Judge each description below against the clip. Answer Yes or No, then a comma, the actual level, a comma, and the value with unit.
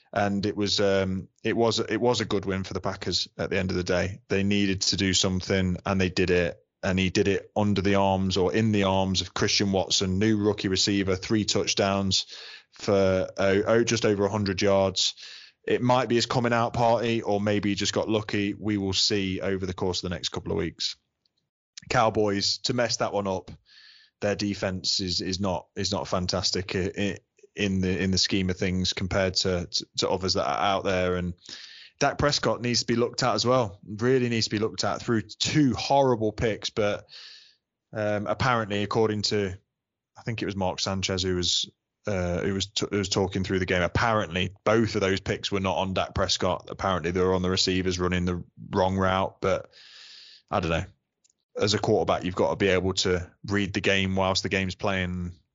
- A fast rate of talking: Yes, fast, 210 wpm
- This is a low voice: Yes, low, 100 Hz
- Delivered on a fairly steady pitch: Yes, narrow, 2.1 semitones